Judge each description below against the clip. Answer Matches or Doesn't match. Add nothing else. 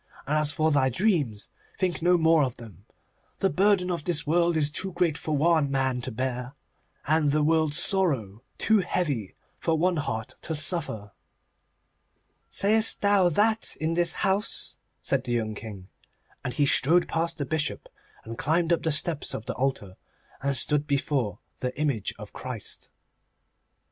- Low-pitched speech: Doesn't match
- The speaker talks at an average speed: Matches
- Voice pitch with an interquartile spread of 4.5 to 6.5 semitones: Matches